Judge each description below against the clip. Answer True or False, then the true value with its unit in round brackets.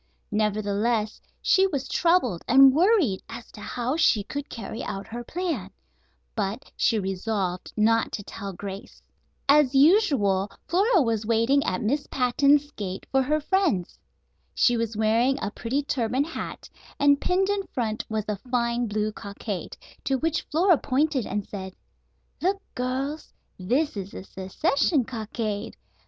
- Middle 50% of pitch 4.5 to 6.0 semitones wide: True (5.5 semitones)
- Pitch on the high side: True (240 Hz)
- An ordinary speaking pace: True (145 wpm)